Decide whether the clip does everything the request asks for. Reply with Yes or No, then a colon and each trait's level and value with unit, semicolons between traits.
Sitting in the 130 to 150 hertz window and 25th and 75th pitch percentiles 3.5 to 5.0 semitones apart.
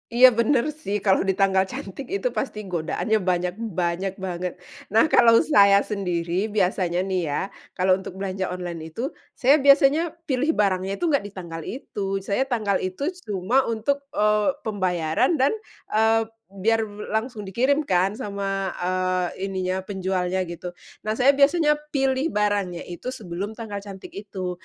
No: high, 200 Hz; average, 4.1 semitones